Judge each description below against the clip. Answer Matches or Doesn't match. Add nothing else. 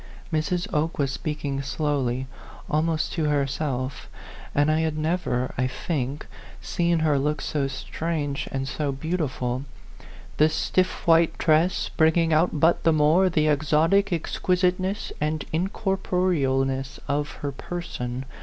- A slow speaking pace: Matches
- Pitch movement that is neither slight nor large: Matches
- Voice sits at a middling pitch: Matches